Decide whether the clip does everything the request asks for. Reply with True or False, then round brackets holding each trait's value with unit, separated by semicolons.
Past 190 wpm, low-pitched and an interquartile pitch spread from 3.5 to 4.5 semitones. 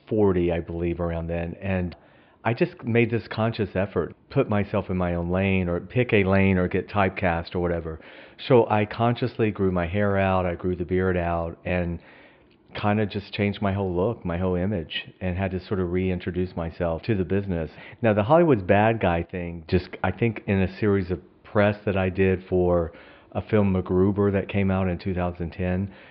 False (200 wpm; 95 Hz; 2.6 semitones)